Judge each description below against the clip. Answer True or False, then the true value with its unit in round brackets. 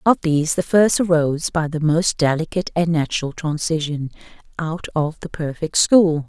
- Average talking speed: True (160 wpm)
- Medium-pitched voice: True (160 Hz)